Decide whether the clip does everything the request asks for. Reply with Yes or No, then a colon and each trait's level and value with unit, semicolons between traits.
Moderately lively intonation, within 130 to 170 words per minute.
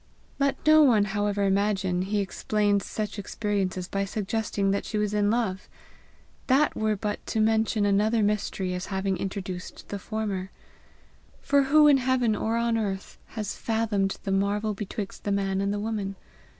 No: narrow, 2.0 semitones; average, 165 wpm